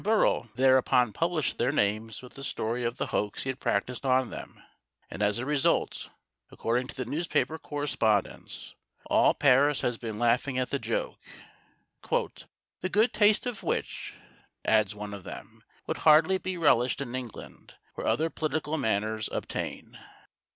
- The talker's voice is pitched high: No, low, 130 Hz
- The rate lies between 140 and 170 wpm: Yes, average, 155 wpm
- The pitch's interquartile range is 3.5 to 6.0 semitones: Yes, wide, 5.4 semitones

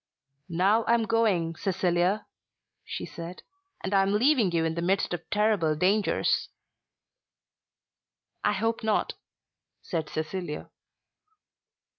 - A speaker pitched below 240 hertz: Yes, high, 190 Hz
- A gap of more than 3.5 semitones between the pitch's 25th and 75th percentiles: Yes, average, 4.0 semitones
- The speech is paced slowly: Yes, slow, 110 wpm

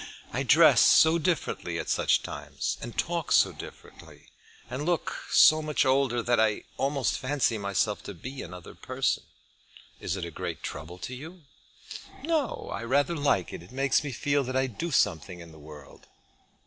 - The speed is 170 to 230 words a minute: Yes, average, 175 wpm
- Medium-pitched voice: No, low, 130 Hz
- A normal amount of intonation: No, wide, 7.0 semitones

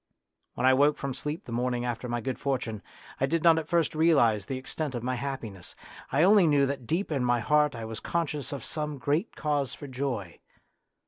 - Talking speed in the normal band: No, fast, 210 wpm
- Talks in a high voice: No, low, 135 Hz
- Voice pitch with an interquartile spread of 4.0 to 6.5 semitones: No, average, 3.6 semitones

